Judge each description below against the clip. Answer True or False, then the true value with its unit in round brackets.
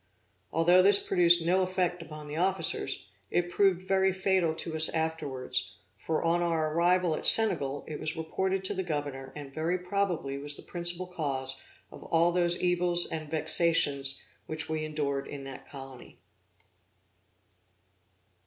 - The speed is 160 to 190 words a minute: False (150 wpm)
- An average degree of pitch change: True (3.2 semitones)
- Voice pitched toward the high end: False (165 Hz)